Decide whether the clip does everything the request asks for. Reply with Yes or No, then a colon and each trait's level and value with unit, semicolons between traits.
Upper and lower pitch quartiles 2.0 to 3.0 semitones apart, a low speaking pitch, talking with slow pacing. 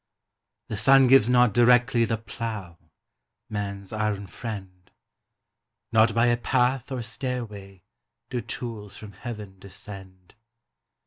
No: average, 3.6 semitones; low, 110 Hz; slow, 115 wpm